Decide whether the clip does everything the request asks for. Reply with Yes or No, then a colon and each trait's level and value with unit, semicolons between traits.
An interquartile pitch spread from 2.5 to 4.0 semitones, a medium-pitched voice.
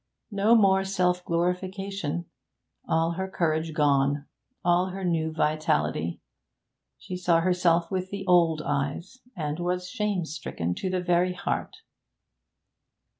Yes: average, 2.8 semitones; medium, 175 Hz